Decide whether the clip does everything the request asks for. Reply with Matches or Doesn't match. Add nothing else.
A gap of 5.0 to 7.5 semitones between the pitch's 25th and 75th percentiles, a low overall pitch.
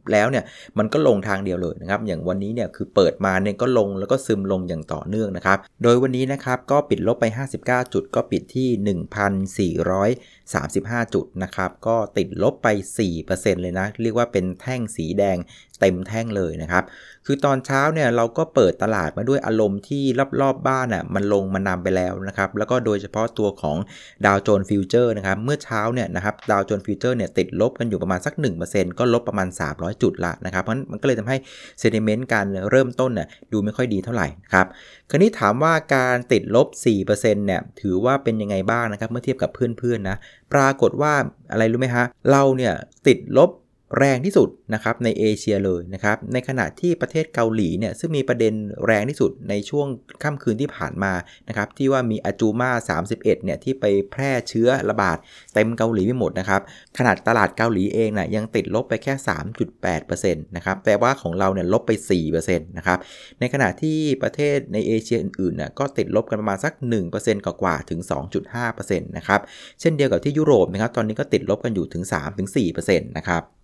Doesn't match